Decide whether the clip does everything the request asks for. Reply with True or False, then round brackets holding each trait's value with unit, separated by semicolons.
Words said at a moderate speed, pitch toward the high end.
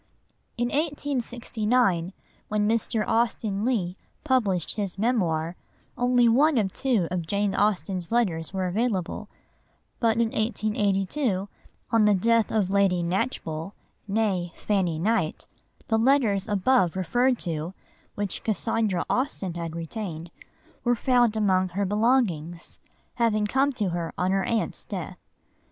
False (125 wpm; 210 Hz)